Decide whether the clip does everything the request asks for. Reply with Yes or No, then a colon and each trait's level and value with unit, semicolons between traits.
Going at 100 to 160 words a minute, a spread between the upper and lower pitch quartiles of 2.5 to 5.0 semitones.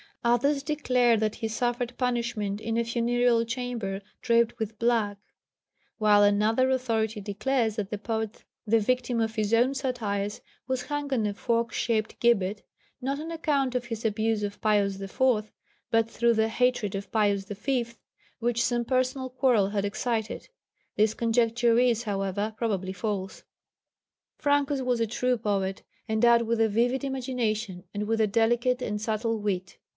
Yes: average, 155 wpm; average, 2.8 semitones